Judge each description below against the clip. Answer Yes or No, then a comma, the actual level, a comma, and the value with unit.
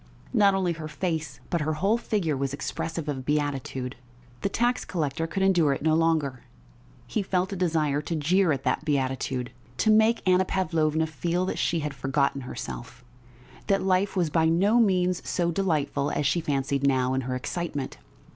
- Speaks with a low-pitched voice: No, medium, 160 Hz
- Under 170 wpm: No, average, 175 wpm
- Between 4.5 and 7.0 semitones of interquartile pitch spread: Yes, average, 4.8 semitones